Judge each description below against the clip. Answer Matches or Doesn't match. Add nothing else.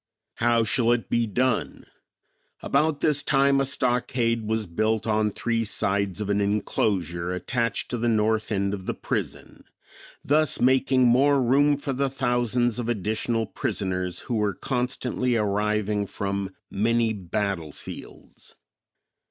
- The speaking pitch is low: Matches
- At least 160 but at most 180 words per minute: Doesn't match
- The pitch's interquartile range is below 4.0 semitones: Matches